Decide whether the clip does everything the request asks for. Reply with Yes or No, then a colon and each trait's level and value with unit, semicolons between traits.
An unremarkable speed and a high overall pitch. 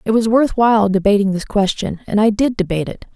No: fast, 230 wpm; high, 210 Hz